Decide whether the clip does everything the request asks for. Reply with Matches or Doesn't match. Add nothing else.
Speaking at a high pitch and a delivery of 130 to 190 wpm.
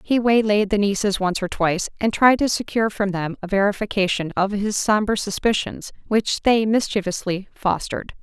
Matches